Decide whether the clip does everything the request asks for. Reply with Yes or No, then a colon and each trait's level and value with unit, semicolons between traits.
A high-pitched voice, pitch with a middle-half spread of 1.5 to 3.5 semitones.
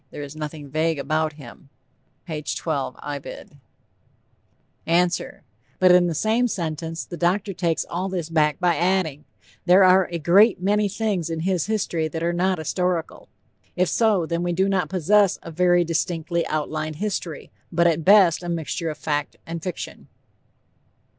No: medium, 170 Hz; average, 2.8 semitones